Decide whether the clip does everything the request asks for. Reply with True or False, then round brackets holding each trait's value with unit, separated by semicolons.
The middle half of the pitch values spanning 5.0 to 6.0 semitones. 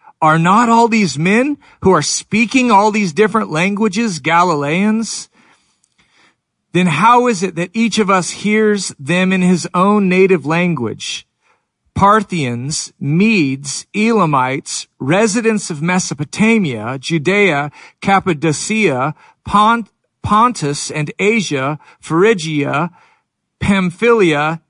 True (5.3 semitones)